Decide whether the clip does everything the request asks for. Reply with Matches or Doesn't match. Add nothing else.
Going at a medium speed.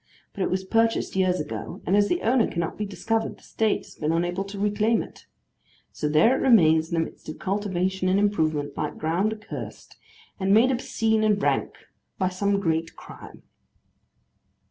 Matches